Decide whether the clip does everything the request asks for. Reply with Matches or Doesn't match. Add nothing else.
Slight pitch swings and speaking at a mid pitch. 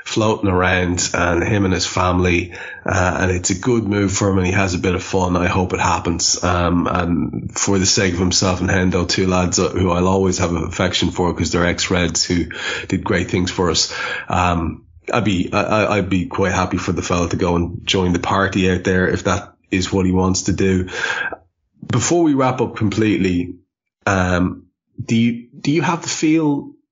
Doesn't match